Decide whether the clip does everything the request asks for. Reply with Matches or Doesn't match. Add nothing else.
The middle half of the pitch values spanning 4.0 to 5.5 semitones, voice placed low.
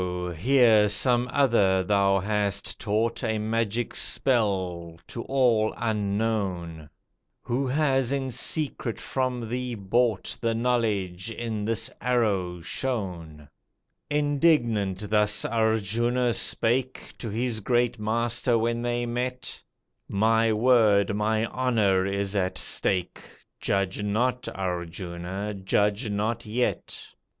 Doesn't match